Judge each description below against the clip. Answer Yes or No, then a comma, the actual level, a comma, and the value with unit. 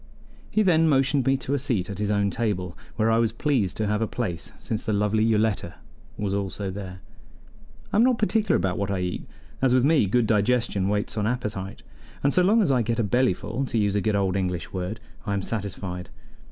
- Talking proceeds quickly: Yes, fast, 220 wpm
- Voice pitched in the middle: No, low, 105 Hz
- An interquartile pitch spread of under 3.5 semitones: No, average, 4.3 semitones